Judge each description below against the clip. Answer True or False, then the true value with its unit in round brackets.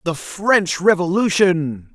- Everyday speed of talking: False (95 wpm)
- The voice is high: False (180 Hz)